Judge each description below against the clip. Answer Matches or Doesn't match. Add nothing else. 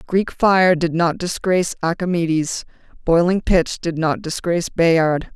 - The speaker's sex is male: Doesn't match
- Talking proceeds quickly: Doesn't match